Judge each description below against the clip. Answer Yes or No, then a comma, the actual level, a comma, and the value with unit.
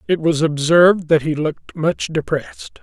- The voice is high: No, medium, 160 Hz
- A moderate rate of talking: Yes, average, 170 wpm